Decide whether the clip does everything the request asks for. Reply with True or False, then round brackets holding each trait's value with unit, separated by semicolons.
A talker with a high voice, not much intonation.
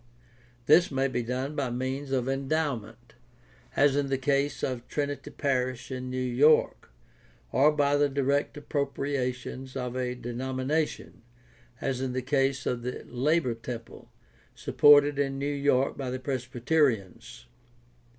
False (135 Hz; 2.2 semitones)